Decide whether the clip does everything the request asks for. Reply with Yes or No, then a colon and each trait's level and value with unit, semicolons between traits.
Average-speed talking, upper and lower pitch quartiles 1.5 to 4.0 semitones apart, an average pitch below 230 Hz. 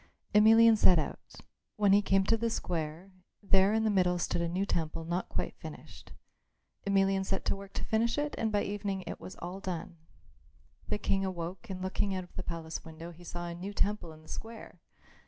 No: fast, 210 wpm; average, 3.0 semitones; high, 190 Hz